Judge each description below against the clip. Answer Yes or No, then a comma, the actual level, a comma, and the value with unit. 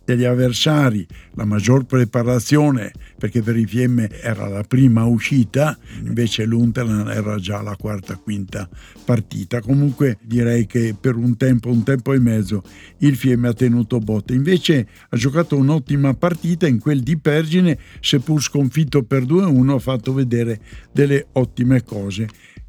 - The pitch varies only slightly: No, average, 4.0 semitones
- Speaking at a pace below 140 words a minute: No, average, 145 wpm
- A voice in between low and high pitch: No, low, 125 Hz